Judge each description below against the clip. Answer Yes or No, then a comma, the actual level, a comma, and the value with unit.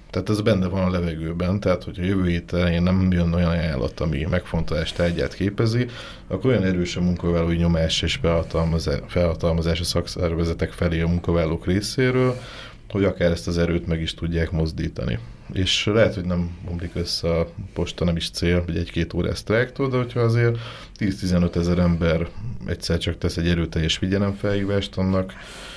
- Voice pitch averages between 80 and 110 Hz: Yes, very low, 85 Hz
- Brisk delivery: Yes, fast, 160 wpm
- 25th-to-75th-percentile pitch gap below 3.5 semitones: Yes, average, 2.7 semitones